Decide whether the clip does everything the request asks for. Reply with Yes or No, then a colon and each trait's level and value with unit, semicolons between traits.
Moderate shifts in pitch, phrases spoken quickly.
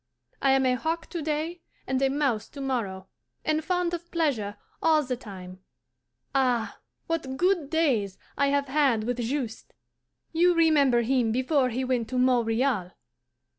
No: average, 4.6 semitones; average, 155 wpm